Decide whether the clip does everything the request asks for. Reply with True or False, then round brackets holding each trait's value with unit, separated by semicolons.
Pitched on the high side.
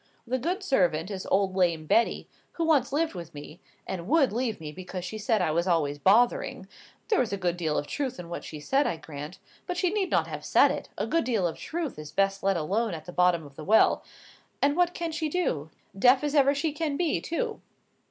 True (205 Hz)